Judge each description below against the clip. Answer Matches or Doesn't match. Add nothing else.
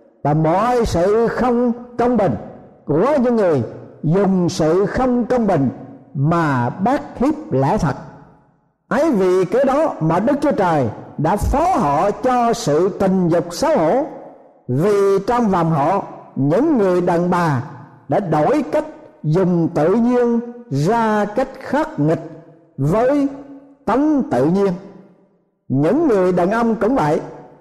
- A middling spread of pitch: Doesn't match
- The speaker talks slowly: Matches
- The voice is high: Matches